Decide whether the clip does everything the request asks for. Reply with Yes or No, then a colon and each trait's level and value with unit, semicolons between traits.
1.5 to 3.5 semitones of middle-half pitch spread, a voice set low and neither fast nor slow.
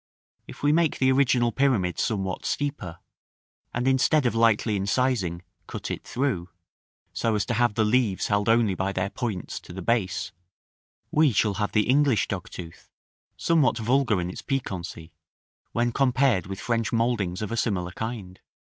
No: average, 4.9 semitones; low, 115 Hz; average, 160 wpm